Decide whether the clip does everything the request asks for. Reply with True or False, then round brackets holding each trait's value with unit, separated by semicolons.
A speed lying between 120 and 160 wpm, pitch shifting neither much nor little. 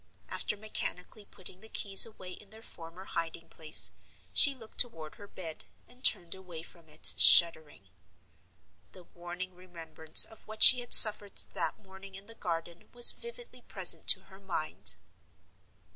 True (155 wpm; 4.3 semitones)